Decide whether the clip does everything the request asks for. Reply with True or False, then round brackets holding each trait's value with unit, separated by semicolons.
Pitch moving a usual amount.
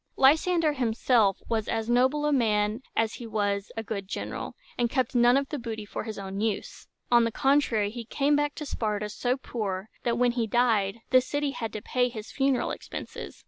True (3.5 semitones)